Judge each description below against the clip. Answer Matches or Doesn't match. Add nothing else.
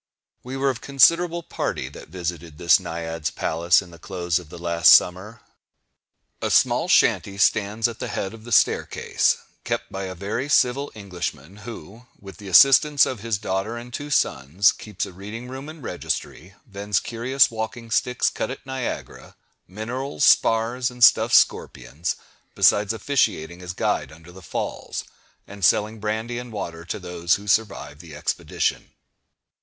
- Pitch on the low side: Matches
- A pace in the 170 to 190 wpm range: Doesn't match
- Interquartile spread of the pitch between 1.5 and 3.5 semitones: Doesn't match